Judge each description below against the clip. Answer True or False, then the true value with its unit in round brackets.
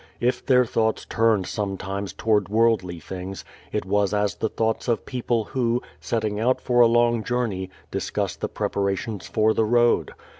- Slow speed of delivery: False (160 wpm)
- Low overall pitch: True (110 Hz)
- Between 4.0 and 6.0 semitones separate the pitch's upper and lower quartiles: False (2.9 semitones)